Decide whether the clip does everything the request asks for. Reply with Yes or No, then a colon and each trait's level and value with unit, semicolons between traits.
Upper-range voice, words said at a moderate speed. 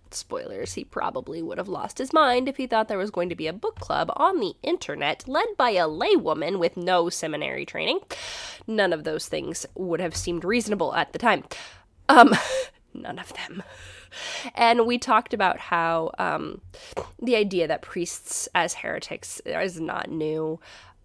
Yes: high, 205 Hz; average, 170 wpm